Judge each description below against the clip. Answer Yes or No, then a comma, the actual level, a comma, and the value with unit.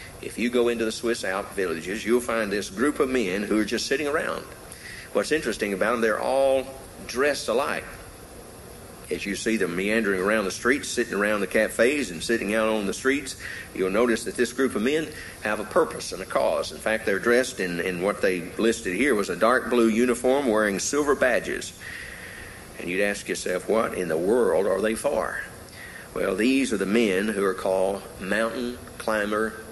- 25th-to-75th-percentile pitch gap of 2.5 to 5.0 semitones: Yes, average, 3.2 semitones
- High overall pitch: No, low, 115 Hz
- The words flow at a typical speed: Yes, average, 195 wpm